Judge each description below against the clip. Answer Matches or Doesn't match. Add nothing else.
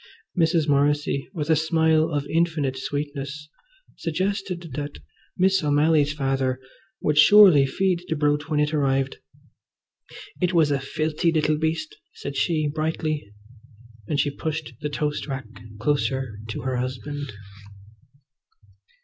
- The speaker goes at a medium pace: Doesn't match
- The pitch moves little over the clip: Matches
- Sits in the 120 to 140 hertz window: Doesn't match